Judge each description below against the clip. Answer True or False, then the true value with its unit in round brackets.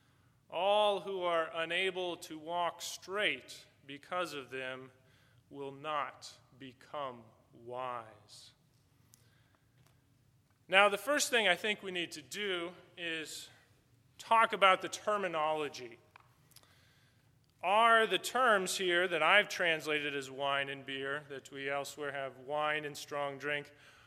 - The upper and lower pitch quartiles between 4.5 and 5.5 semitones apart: True (5.1 semitones)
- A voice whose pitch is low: False (145 Hz)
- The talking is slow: True (120 wpm)